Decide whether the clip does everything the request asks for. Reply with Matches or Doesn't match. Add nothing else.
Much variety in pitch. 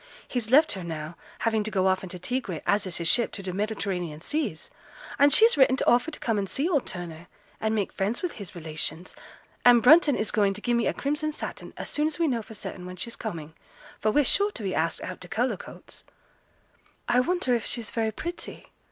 Matches